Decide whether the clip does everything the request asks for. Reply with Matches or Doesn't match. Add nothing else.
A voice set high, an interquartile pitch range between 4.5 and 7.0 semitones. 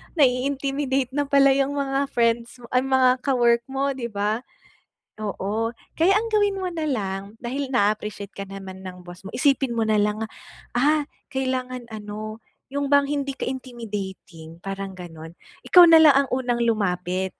Matches